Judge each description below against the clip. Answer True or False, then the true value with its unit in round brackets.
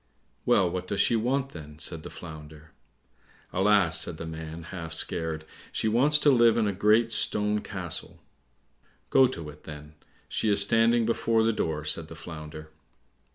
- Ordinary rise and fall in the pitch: False (6.1 semitones)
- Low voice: True (90 Hz)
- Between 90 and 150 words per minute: False (165 wpm)